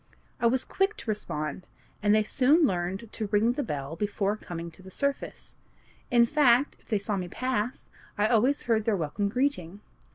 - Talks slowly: No, average, 185 wpm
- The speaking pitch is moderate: No, high, 215 Hz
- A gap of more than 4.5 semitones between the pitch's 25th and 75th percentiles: Yes, average, 4.9 semitones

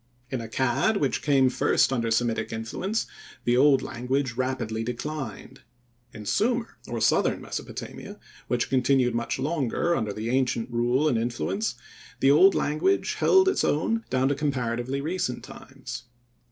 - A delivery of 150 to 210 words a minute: No, average, 140 wpm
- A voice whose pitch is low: Yes, low, 130 Hz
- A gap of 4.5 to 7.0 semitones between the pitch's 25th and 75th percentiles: No, average, 3.7 semitones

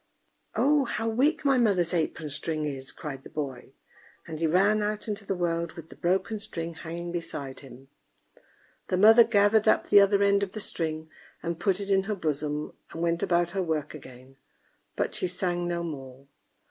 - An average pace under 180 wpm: No, average, 185 wpm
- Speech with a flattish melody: No, average, 4.5 semitones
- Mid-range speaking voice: Yes, medium, 175 Hz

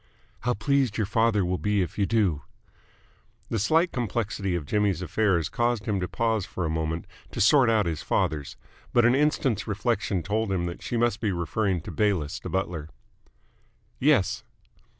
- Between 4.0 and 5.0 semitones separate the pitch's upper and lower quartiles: Yes, average, 4.5 semitones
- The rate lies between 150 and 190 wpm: Yes, average, 170 wpm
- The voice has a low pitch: Yes, low, 105 Hz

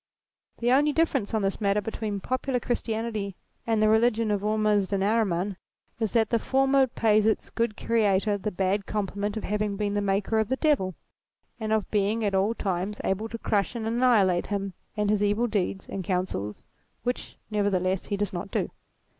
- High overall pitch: Yes, high, 210 Hz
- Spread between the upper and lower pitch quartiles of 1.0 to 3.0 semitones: Yes, narrow, 2.4 semitones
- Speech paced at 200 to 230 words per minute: No, average, 190 wpm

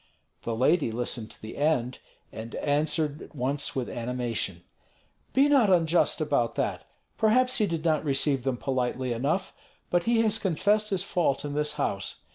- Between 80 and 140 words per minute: No, average, 165 wpm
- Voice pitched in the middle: Yes, medium, 150 Hz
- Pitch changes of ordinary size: No, wide, 6.4 semitones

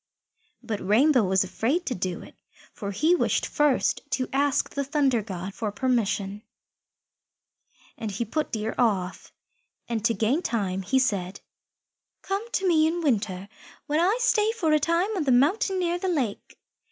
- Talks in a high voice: Yes, very high, 255 Hz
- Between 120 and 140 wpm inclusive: No, average, 165 wpm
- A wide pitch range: Yes, wide, 7.6 semitones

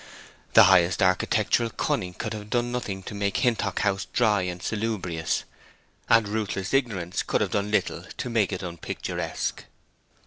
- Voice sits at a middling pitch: No, low, 100 Hz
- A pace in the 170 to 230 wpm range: No, average, 150 wpm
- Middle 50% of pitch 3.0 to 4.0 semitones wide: Yes, average, 3.3 semitones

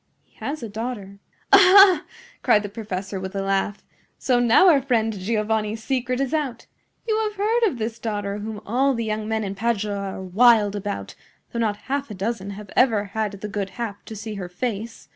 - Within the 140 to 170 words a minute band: No, average, 200 wpm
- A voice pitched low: No, high, 220 Hz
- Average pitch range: Yes, average, 3.6 semitones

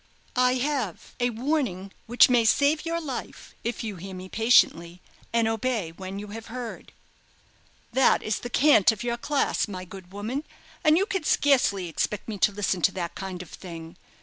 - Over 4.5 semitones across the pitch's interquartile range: Yes, average, 5.2 semitones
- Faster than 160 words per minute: Yes, average, 180 wpm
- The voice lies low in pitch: No, high, 220 Hz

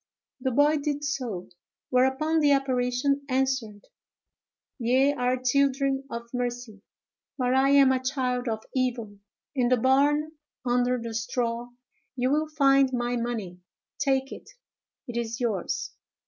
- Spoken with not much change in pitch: Yes, narrow, 2.2 semitones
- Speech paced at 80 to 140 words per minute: Yes, slow, 135 wpm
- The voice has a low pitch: No, very high, 255 Hz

